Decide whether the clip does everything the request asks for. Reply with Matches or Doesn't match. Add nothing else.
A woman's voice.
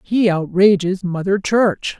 Matches